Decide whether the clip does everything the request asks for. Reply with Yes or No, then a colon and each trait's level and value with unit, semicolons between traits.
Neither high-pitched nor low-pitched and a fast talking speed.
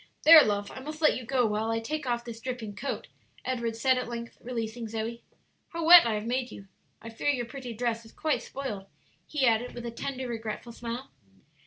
No: high, 235 Hz; fast, 210 wpm